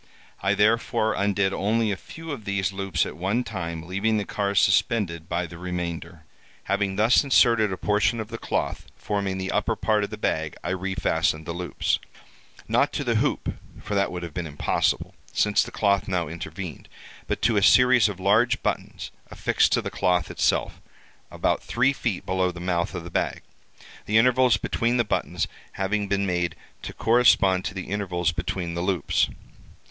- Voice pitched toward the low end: Yes, very low, 95 Hz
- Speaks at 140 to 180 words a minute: Yes, average, 175 wpm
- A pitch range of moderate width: Yes, average, 3.4 semitones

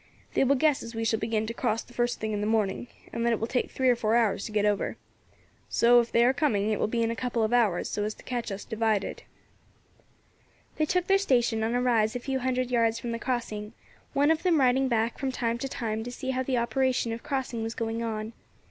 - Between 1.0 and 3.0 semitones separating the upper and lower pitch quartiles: Yes, narrow, 2.4 semitones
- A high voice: Yes, high, 235 Hz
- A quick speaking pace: Yes, fast, 255 wpm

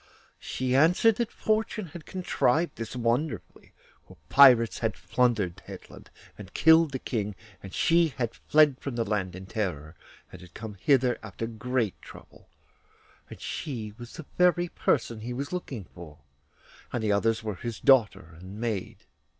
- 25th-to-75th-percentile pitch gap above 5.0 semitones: Yes, wide, 5.6 semitones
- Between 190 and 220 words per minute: No, average, 160 wpm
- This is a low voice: Yes, low, 120 Hz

